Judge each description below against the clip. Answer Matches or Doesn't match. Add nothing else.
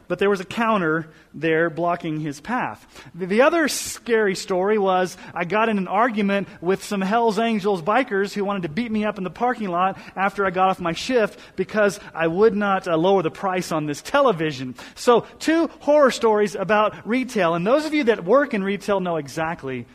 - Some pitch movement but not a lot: Matches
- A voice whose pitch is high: Matches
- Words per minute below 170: Doesn't match